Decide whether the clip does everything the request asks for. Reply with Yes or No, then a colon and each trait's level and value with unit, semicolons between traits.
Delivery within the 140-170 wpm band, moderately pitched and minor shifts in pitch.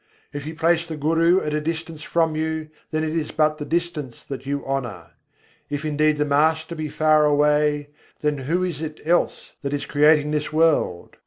No: average, 190 wpm; medium, 155 Hz; narrow, 1.5 semitones